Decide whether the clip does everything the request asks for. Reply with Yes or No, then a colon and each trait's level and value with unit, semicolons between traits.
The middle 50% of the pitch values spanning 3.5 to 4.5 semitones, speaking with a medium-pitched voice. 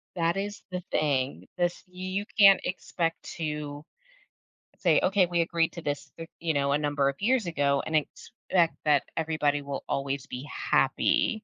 Yes: average, 3.8 semitones; medium, 160 Hz